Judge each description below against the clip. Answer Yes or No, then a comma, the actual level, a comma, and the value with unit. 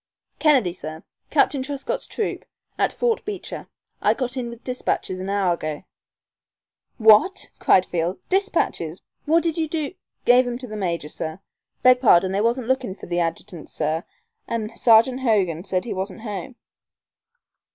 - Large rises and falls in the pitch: Yes, wide, 6.2 semitones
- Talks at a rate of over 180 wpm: No, average, 160 wpm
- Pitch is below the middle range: No, high, 225 Hz